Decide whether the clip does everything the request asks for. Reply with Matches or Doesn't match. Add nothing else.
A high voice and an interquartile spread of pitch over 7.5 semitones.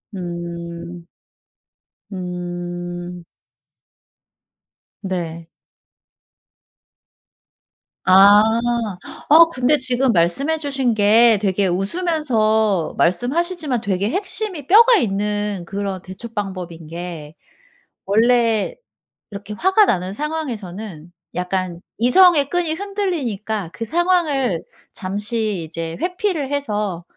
Matches